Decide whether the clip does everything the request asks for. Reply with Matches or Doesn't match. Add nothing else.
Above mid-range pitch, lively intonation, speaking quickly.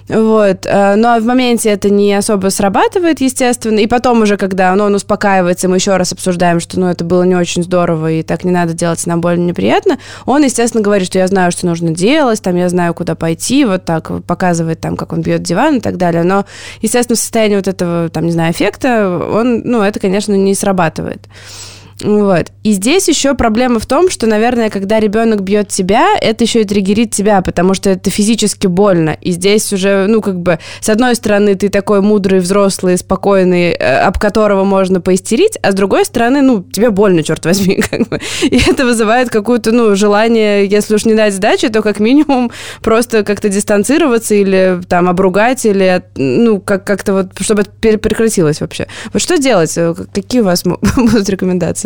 Doesn't match